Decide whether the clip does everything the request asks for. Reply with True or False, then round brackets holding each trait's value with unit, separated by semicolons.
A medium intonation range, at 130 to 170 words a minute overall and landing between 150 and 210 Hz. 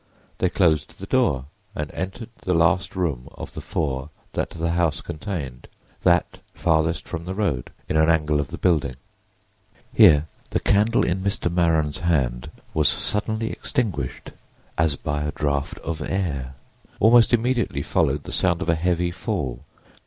False (4.0 semitones; 155 wpm; 80 Hz)